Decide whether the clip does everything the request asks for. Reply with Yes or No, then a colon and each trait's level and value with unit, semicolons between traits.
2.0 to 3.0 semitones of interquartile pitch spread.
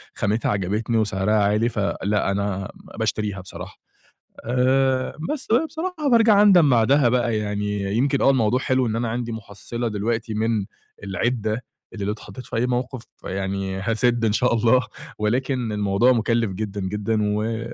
No: average, 3.4 semitones